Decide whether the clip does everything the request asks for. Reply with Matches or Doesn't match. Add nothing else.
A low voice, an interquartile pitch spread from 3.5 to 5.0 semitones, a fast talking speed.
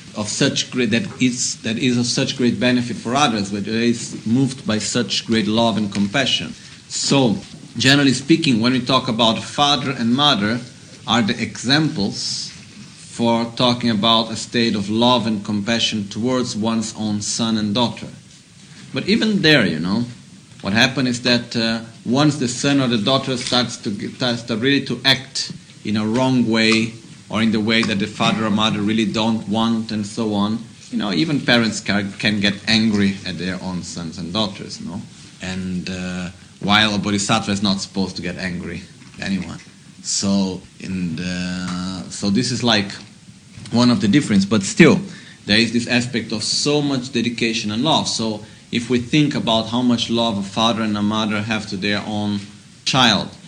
Doesn't match